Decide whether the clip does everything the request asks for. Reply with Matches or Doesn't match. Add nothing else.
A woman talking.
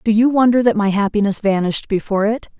Matches